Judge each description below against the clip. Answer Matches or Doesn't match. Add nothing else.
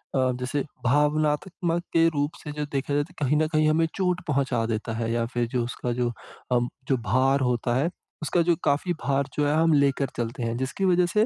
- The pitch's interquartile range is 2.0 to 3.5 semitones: Doesn't match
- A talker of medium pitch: Matches